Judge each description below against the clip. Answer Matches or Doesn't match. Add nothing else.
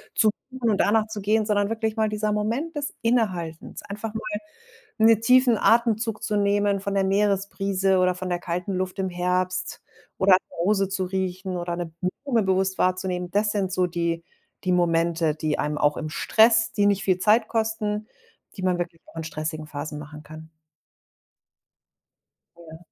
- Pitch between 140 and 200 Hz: Matches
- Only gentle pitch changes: Doesn't match